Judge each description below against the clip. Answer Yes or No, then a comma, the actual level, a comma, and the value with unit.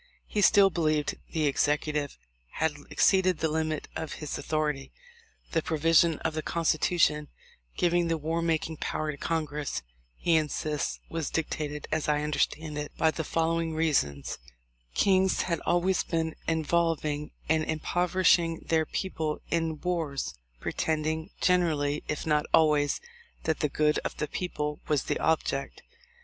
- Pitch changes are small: Yes, narrow, 1.7 semitones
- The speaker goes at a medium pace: Yes, average, 145 wpm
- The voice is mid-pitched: Yes, medium, 160 Hz